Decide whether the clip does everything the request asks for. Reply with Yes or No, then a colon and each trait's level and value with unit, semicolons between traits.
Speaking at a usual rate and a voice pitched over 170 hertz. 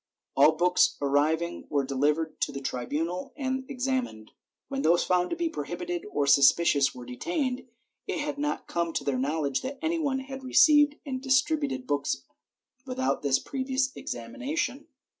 Yes: average, 155 wpm; medium, 185 Hz